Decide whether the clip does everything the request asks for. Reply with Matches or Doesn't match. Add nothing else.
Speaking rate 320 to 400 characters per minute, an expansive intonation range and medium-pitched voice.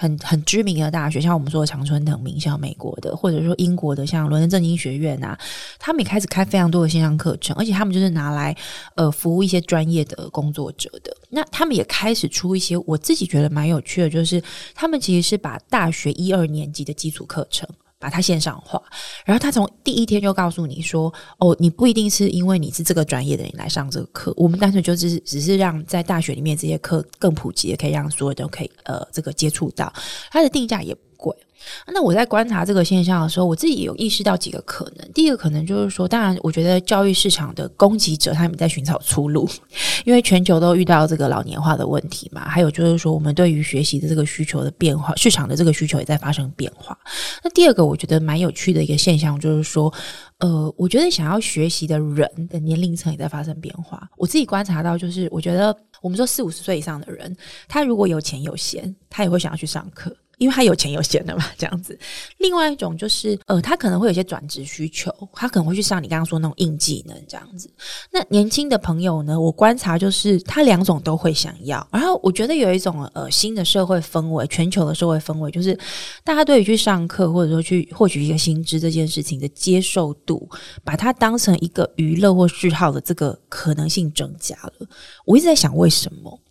Doesn't match